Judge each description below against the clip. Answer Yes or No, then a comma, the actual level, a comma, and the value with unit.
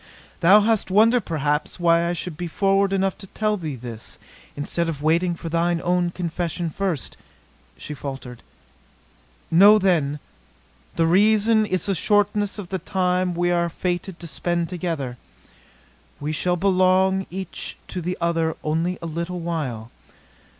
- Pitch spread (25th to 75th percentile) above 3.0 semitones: No, average, 2.7 semitones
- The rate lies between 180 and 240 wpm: No, average, 150 wpm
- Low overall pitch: No, medium, 175 Hz